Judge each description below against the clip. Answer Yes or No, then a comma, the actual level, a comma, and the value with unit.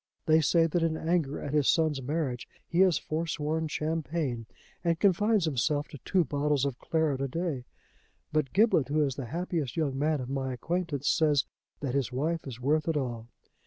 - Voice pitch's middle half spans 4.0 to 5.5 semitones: No, average, 3.3 semitones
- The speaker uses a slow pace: No, average, 185 wpm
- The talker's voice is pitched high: No, medium, 150 Hz